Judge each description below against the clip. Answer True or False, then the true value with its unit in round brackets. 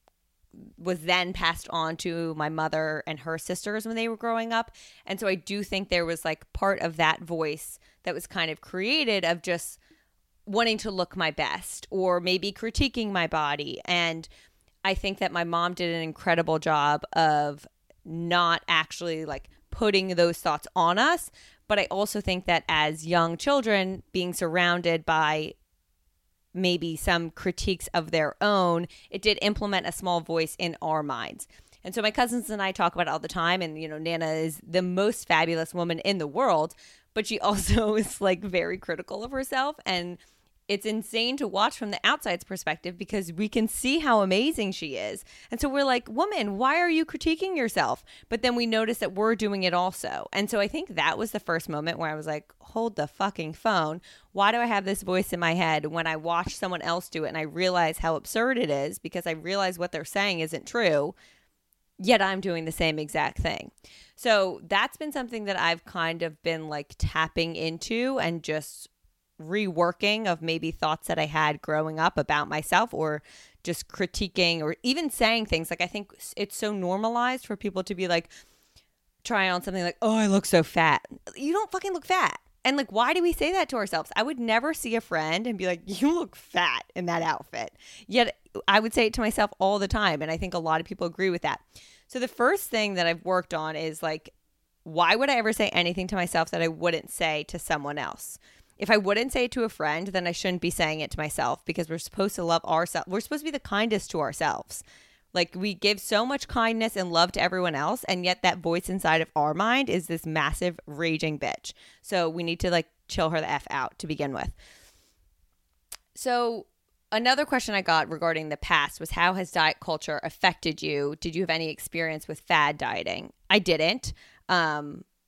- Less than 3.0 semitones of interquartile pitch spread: False (4.4 semitones)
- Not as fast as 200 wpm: False (205 wpm)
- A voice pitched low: False (180 Hz)